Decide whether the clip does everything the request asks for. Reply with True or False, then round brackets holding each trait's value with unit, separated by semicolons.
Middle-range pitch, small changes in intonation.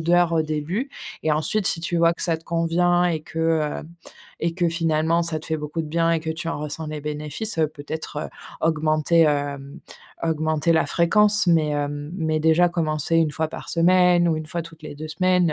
True (160 Hz; 1.7 semitones)